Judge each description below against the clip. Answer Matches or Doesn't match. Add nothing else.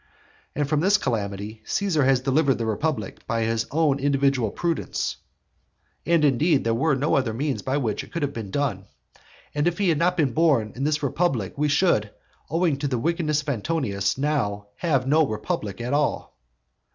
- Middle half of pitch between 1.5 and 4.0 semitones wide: Doesn't match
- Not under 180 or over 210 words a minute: Matches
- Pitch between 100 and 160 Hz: Matches